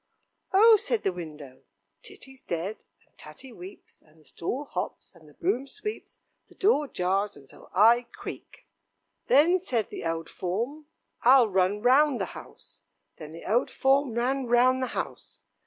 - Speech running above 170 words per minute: No, average, 160 wpm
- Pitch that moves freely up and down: Yes, wide, 7.3 semitones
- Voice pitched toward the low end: No, high, 235 Hz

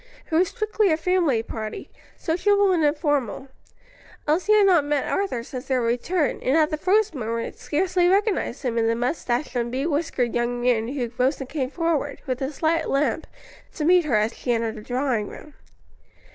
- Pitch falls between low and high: No, very high, 290 Hz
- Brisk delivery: No, average, 185 wpm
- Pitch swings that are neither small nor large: No, wide, 5.8 semitones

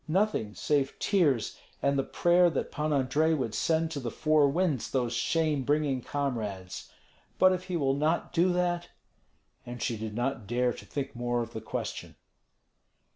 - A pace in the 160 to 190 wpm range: Yes, average, 170 wpm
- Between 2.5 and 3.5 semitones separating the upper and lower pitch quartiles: No, average, 5.0 semitones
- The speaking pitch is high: No, medium, 140 Hz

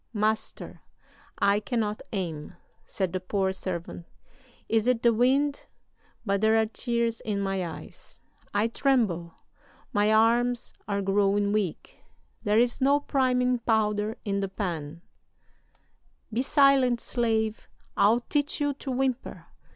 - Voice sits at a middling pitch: No, high, 220 Hz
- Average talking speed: No, slow, 130 wpm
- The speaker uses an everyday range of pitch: Yes, average, 3.6 semitones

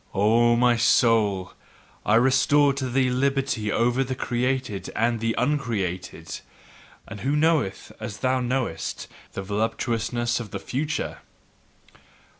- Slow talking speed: Yes, slow, 120 wpm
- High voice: No, low, 120 Hz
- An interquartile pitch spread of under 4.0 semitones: Yes, average, 3.3 semitones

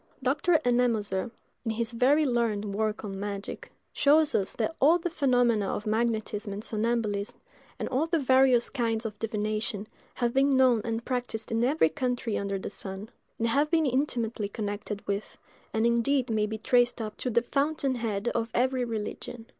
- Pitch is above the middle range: Yes, high, 235 Hz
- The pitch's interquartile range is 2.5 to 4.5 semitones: Yes, average, 3.3 semitones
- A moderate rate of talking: Yes, average, 170 wpm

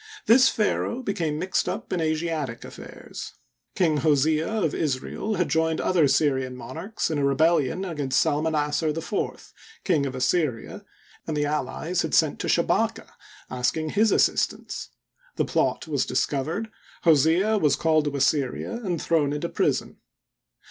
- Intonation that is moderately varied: Yes, average, 3.3 semitones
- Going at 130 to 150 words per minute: Yes, average, 140 wpm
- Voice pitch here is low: No, medium, 155 Hz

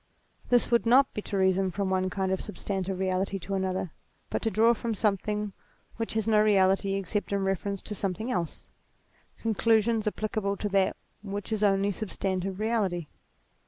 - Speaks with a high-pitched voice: Yes, high, 200 Hz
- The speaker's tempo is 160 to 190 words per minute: Yes, average, 170 wpm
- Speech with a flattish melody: Yes, narrow, 2.3 semitones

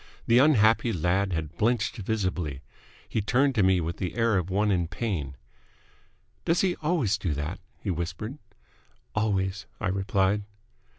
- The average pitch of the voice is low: Yes, low, 100 Hz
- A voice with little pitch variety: No, average, 4.3 semitones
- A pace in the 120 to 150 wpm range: Yes, average, 145 wpm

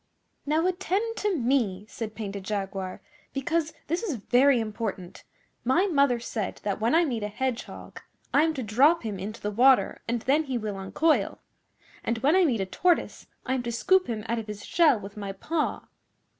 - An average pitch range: No, wide, 6.6 semitones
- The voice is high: Yes, high, 240 Hz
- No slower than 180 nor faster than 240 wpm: Yes, average, 190 wpm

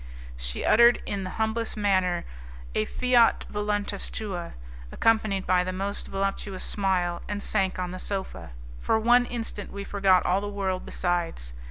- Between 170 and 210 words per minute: No, average, 155 wpm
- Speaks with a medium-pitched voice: No, high, 195 Hz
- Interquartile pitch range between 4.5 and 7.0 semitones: No, narrow, 2.4 semitones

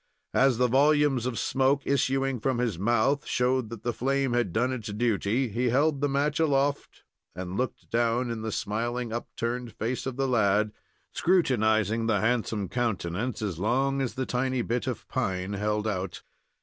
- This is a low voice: Yes, low, 120 Hz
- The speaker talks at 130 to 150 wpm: No, average, 170 wpm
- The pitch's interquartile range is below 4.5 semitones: Yes, average, 3.5 semitones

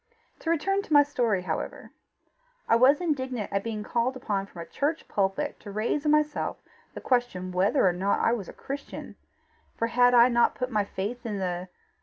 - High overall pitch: Yes, high, 235 Hz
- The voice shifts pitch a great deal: Yes, wide, 5.8 semitones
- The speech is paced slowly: No, average, 195 wpm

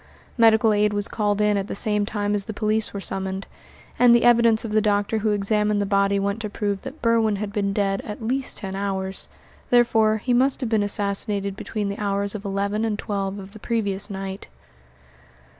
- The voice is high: Yes, high, 205 Hz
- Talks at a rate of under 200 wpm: No, fast, 205 wpm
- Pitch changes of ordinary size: No, narrow, 1.7 semitones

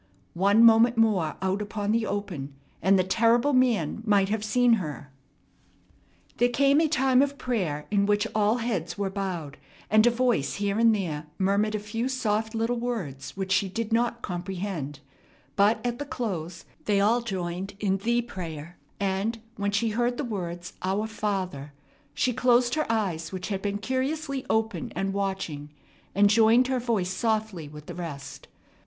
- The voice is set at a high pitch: Yes, high, 205 Hz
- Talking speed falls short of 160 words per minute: No, average, 170 wpm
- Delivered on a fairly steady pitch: No, average, 4.0 semitones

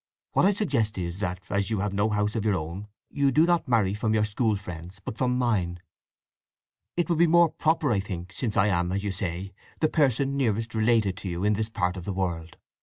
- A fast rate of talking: Yes, fast, 230 wpm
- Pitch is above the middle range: No, low, 105 Hz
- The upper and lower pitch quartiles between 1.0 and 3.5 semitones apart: No, average, 4.7 semitones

